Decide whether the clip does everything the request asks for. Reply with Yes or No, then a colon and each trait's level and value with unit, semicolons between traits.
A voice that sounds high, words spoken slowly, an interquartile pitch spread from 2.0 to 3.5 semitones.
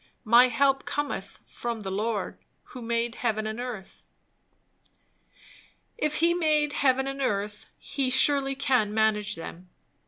No: high, 240 Hz; slow, 130 wpm; average, 4.1 semitones